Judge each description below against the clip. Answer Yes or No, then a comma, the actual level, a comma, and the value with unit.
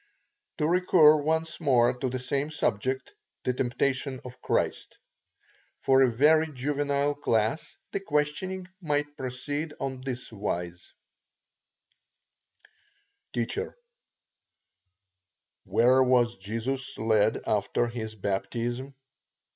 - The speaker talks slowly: Yes, slow, 100 wpm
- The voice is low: Yes, low, 130 Hz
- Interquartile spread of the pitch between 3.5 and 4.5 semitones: Yes, average, 3.8 semitones